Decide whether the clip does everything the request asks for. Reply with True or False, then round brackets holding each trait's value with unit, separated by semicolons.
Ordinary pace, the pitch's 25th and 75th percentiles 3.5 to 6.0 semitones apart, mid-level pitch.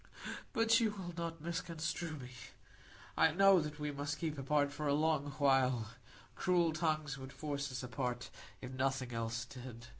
True (160 wpm; 3.9 semitones; 145 Hz)